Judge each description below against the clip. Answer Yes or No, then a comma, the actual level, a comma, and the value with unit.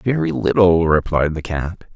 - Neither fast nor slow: Yes, average, 155 wpm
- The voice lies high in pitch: No, very low, 85 Hz